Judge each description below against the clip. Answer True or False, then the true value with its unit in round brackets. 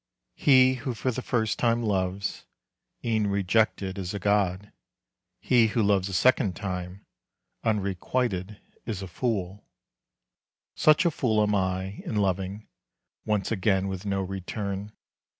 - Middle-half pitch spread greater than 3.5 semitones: False (2.8 semitones)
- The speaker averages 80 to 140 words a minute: True (135 wpm)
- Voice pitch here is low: True (100 Hz)